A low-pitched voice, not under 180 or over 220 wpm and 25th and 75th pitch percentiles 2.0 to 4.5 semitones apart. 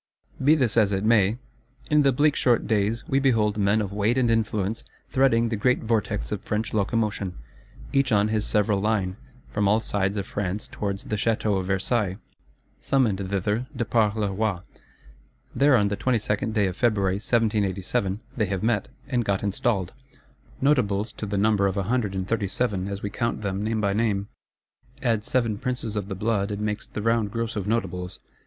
Yes: low, 105 Hz; average, 190 wpm; narrow, 2.5 semitones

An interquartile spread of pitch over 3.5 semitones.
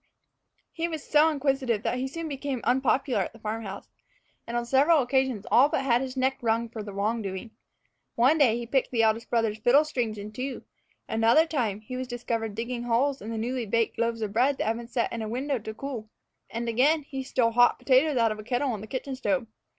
No: average, 3.0 semitones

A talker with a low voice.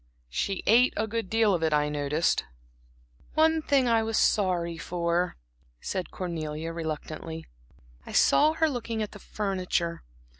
No: medium, 185 Hz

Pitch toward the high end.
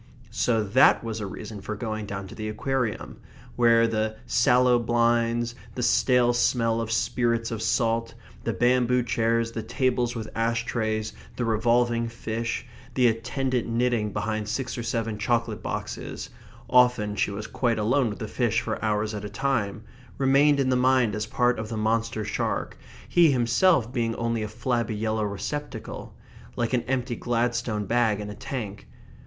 No: low, 115 Hz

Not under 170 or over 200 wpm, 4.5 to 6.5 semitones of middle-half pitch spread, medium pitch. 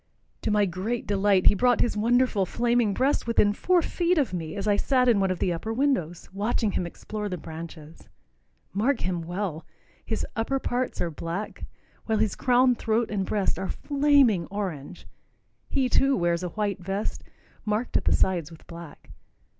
No: average, 180 wpm; average, 5.1 semitones; high, 205 Hz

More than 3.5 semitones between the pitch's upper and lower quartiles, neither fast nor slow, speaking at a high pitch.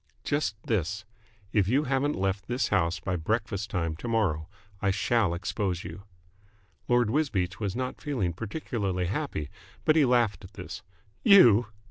No: average, 4.9 semitones; average, 150 wpm; low, 105 Hz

